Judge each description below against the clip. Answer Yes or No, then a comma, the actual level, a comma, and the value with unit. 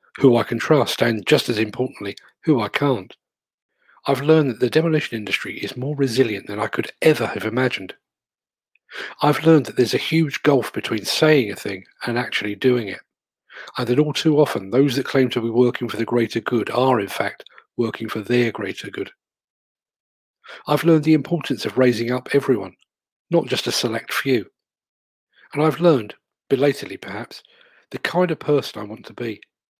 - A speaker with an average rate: Yes, average, 180 wpm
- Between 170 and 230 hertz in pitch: No, low, 130 Hz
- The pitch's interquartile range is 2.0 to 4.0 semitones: No, average, 4.5 semitones